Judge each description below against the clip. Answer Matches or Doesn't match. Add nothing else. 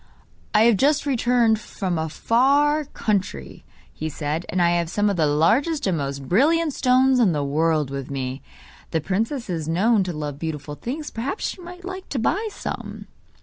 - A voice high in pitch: Matches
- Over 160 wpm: Matches